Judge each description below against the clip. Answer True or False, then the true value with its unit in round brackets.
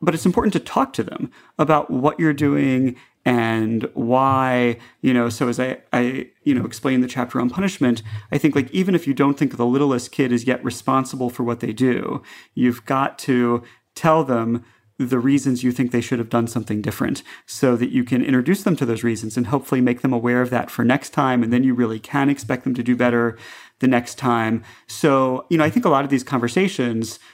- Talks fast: True (220 wpm)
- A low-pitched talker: True (125 Hz)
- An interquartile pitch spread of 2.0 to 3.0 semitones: True (2.4 semitones)